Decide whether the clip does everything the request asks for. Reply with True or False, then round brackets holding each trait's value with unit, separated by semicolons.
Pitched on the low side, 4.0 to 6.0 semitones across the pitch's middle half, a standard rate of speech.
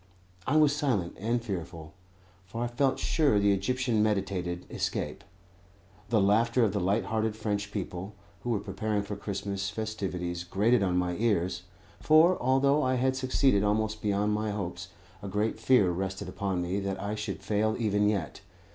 False (105 Hz; 3.2 semitones; 165 wpm)